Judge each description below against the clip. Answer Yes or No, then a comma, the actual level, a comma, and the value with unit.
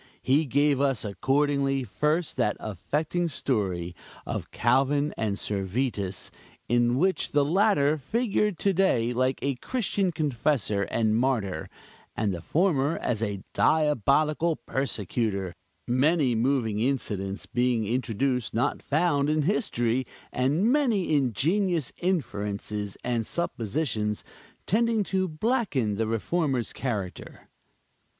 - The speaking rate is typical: No, slow, 115 wpm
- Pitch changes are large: Yes, wide, 5.9 semitones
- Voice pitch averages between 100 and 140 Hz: Yes, low, 135 Hz